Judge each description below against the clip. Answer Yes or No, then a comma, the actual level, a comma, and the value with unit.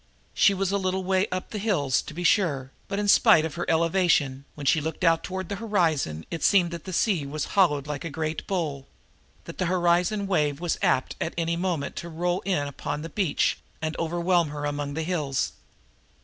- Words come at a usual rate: No, fast, 210 wpm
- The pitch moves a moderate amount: Yes, average, 3.9 semitones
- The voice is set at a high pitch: No, medium, 170 Hz